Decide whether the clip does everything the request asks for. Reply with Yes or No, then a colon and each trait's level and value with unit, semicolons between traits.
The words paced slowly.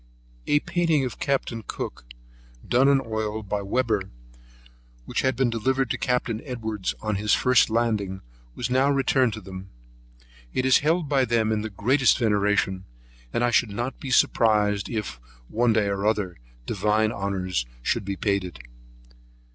No: average, 165 wpm